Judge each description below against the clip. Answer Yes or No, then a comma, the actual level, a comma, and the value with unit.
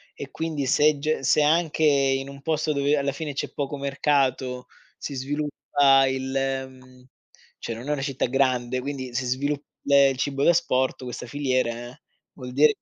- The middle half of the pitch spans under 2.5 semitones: Yes, narrow, 1.9 semitones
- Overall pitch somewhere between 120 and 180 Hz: Yes, low, 135 Hz